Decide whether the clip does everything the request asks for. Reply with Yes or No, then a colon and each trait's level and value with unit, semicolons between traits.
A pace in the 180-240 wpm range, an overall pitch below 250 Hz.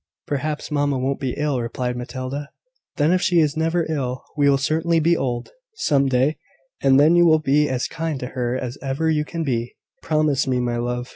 Yes: fast, 205 wpm; medium, 140 Hz